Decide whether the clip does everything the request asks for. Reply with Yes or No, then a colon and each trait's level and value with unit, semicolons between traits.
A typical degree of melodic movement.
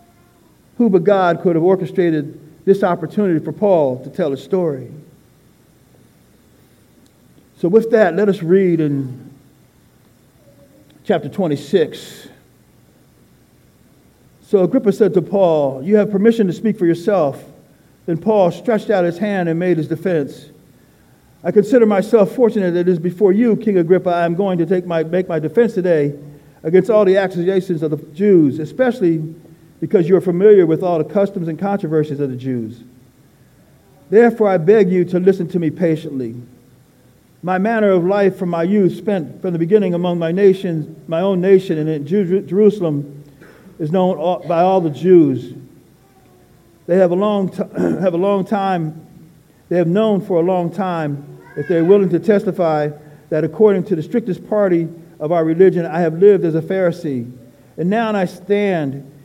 Yes: average, 3.9 semitones